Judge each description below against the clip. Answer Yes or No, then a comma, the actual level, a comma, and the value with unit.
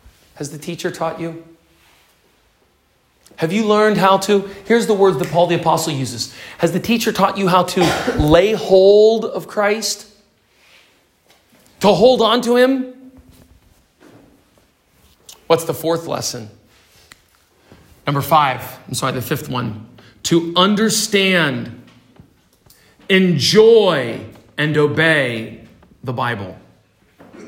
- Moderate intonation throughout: No, wide, 7.9 semitones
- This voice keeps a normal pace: No, slow, 115 wpm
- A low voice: No, medium, 165 Hz